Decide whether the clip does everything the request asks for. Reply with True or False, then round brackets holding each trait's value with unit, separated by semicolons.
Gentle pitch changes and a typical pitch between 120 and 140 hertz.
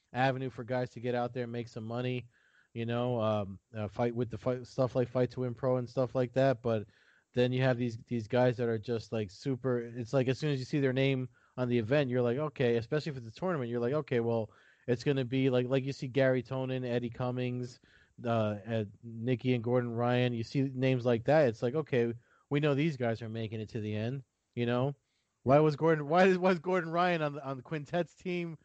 True (2.2 semitones; 125 Hz)